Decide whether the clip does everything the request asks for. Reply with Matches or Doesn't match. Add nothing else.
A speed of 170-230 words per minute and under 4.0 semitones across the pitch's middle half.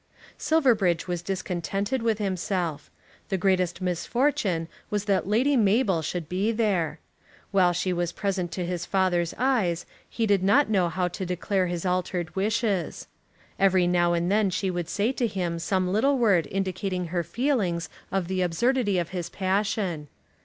Doesn't match